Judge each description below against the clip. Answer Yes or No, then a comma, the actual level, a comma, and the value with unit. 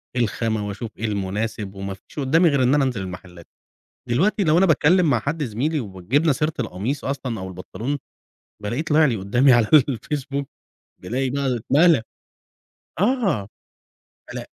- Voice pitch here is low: Yes, low, 130 Hz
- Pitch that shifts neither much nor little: No, wide, 5.8 semitones